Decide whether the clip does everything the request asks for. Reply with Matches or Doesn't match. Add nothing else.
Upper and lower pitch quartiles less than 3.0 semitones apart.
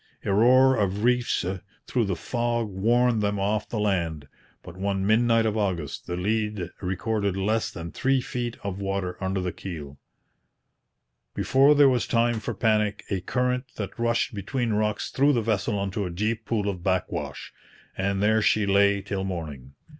Doesn't match